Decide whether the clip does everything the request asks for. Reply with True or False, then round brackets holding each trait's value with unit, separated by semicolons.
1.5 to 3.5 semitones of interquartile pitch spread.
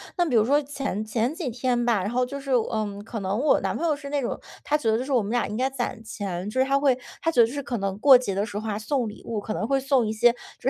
False (4.0 semitones)